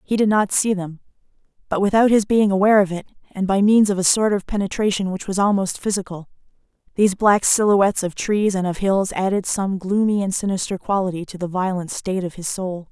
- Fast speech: Yes, fast, 210 wpm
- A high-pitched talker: Yes, high, 195 Hz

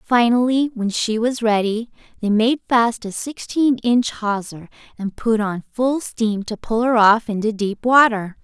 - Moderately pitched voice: No, high, 225 Hz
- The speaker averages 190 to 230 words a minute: No, average, 170 wpm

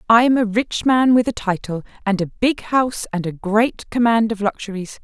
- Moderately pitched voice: No, high, 220 Hz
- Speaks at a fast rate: Yes, fast, 215 wpm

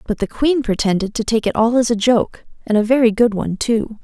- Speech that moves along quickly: Yes, fast, 255 wpm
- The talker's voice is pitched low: No, high, 225 Hz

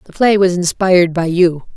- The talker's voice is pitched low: No, medium, 180 Hz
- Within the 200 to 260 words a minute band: Yes, fast, 205 wpm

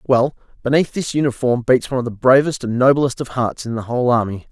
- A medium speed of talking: No, fast, 215 wpm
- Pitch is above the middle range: No, low, 125 Hz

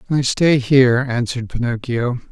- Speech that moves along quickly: No, slow, 130 wpm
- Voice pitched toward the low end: Yes, low, 125 Hz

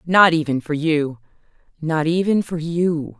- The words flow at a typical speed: No, slow, 130 wpm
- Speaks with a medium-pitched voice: Yes, medium, 160 Hz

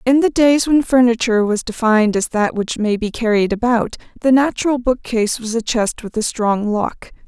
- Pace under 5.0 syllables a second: No, 5.2 syllables/s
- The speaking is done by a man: No, female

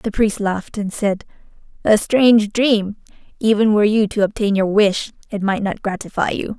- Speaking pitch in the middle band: No, high, 210 Hz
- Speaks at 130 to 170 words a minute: No, average, 180 wpm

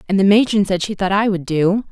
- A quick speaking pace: Yes, fast, 280 wpm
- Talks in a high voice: Yes, high, 195 Hz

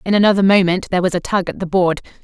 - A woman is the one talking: Yes, female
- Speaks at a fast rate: Yes, fast, 270 wpm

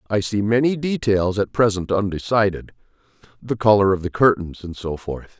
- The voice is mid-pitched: No, low, 105 Hz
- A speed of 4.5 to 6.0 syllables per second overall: Yes, 5.1 syllables/s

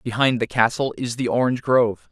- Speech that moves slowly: No, average, 200 wpm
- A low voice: Yes, low, 125 Hz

